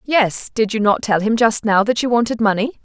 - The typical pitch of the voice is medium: No, high, 225 Hz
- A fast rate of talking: Yes, fast, 255 wpm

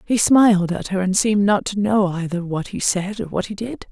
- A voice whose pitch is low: No, high, 200 Hz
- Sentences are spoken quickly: Yes, fast, 260 wpm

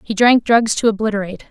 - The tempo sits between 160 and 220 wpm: Yes, average, 200 wpm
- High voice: Yes, high, 215 Hz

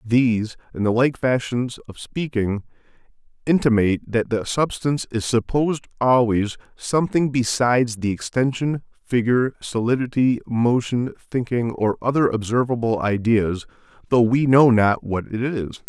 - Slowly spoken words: Yes, slow, 125 wpm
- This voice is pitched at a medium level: No, low, 120 Hz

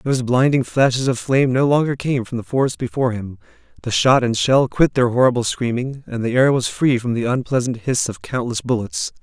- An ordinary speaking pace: No, fast, 215 wpm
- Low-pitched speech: Yes, low, 125 Hz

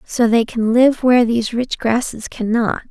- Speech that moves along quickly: No, average, 185 wpm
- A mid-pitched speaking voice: No, high, 235 Hz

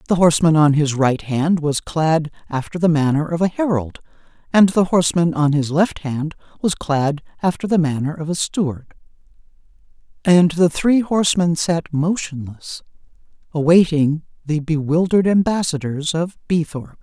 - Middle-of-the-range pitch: Yes, medium, 160 Hz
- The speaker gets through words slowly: No, average, 145 wpm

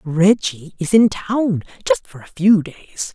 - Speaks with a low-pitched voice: No, medium, 180 Hz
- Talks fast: No, average, 170 wpm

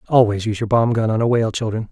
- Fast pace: Yes, fast, 285 wpm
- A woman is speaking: No, male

